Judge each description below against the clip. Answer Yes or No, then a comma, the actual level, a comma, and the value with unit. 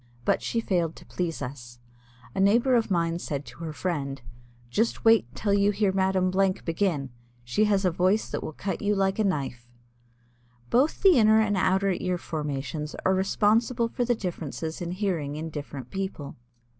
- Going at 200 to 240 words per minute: No, average, 180 wpm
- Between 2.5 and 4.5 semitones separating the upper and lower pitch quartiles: No, average, 5.1 semitones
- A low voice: No, medium, 185 Hz